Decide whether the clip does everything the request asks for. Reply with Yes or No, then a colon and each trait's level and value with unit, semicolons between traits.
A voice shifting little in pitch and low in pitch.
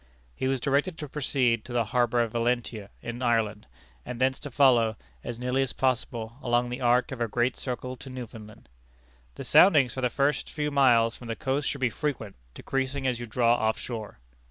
Yes: narrow, 2.3 semitones; low, 125 Hz